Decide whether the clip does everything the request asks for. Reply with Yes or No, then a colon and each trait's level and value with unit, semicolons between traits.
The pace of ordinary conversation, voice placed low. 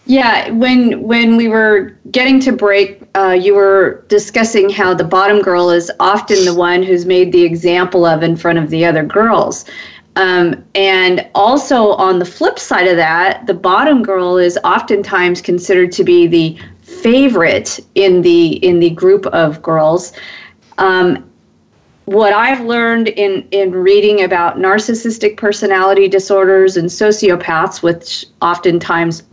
No: average, 145 wpm; high, 190 Hz